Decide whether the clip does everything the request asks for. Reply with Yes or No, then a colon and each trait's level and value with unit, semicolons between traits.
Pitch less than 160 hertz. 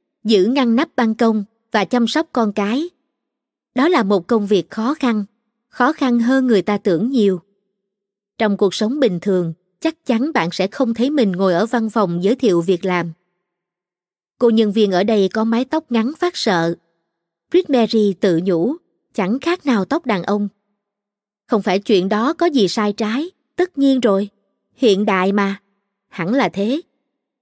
No: high, 215 Hz